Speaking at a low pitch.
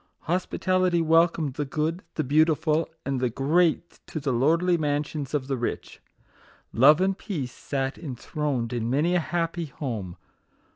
No: medium, 150 Hz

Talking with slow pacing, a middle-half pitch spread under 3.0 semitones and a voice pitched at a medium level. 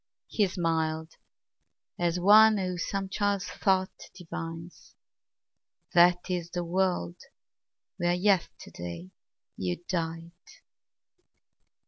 Yes: slow, 85 wpm; narrow, 2.6 semitones; medium, 175 Hz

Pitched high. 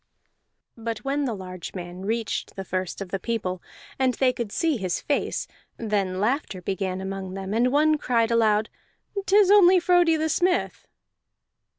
Yes: high, 225 Hz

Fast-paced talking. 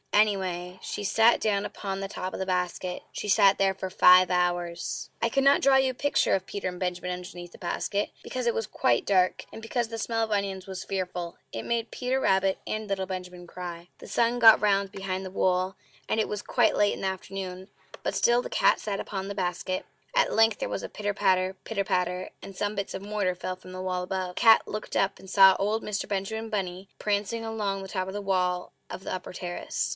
Yes: fast, 225 wpm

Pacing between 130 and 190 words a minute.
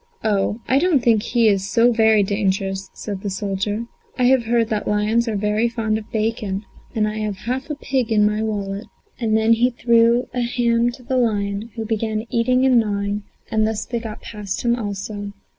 No: average, 200 wpm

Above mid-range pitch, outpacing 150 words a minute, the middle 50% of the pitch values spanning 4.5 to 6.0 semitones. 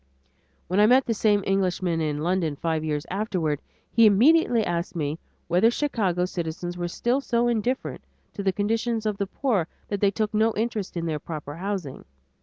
Yes: high, 195 Hz; average, 180 wpm; average, 4.8 semitones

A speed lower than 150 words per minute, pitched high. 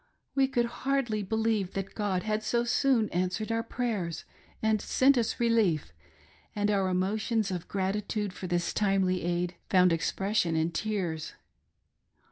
Yes: average, 140 wpm; high, 205 Hz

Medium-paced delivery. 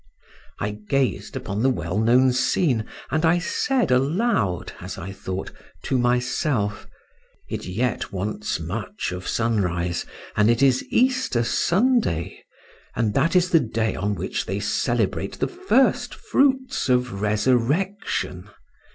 No: slow, 130 wpm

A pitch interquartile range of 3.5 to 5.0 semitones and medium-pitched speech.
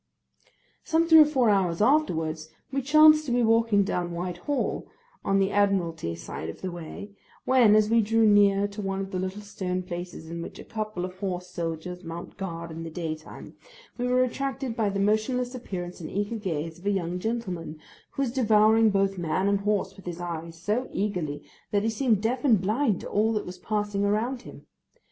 No: average, 4.3 semitones; high, 200 Hz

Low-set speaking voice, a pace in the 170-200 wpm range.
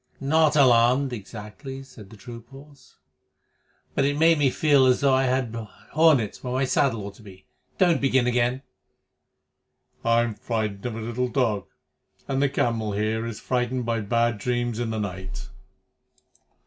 No: low, 120 Hz; average, 160 wpm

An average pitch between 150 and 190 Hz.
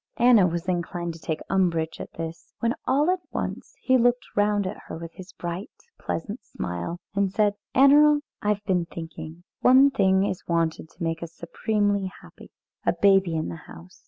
Yes: medium, 185 Hz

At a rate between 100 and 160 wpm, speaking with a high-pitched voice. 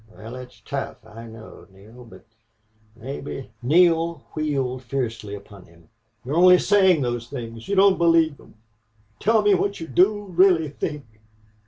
No: average, 155 wpm; medium, 140 Hz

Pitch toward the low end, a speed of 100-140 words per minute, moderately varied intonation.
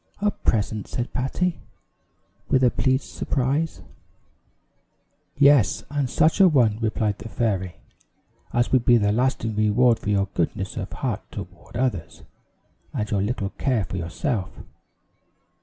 Yes: low, 115 Hz; slow, 135 wpm; average, 4.2 semitones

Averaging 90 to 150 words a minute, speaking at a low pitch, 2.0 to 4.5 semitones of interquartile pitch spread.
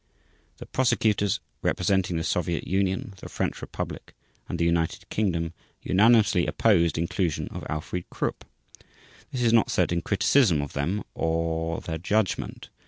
Yes: average, 140 wpm; very low, 90 Hz; average, 3.7 semitones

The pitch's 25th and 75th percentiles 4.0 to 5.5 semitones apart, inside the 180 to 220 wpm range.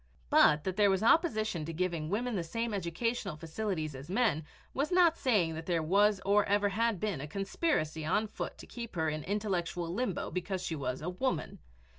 Yes: average, 5.1 semitones; average, 195 wpm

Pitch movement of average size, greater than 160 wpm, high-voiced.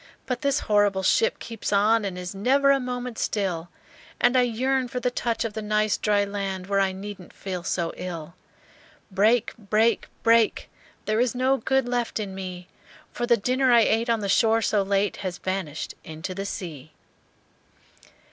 Yes: average, 4.0 semitones; average, 175 wpm; high, 210 Hz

